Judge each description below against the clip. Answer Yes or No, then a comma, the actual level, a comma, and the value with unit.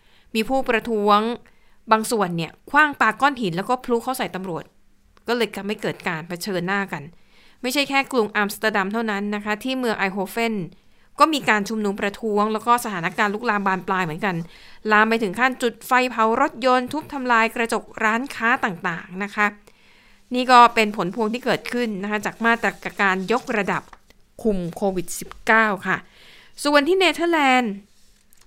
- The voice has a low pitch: No, high, 220 Hz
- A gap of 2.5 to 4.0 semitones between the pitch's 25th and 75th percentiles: Yes, average, 3.4 semitones